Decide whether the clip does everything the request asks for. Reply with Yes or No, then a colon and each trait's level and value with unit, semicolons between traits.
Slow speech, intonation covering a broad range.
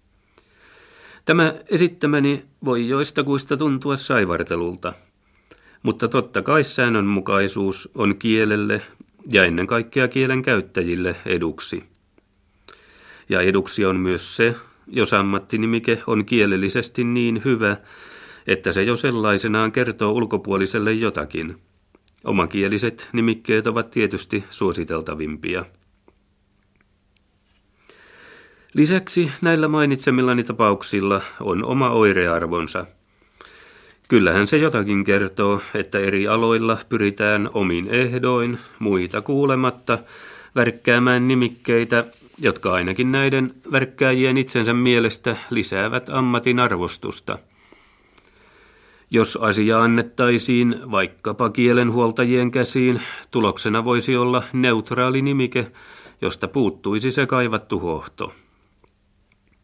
No: slow, 90 wpm; average, 3.9 semitones